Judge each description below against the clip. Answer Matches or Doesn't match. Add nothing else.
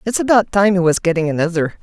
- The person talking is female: Matches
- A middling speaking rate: Doesn't match